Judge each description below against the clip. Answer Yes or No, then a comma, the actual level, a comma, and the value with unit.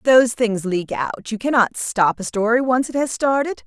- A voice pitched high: Yes, high, 230 Hz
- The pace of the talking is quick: Yes, fast, 215 wpm